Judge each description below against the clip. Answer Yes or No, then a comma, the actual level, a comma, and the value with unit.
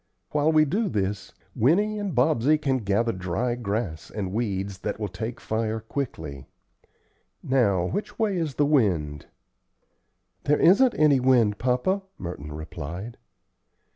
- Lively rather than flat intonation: Yes, wide, 7.4 semitones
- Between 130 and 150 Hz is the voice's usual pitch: No, low, 115 Hz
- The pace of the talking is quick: No, slow, 135 wpm